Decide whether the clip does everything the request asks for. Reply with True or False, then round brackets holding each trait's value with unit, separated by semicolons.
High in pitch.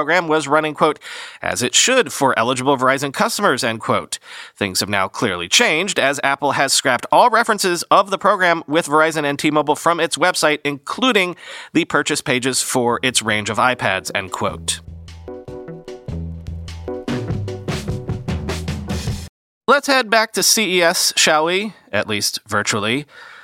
False (140 Hz)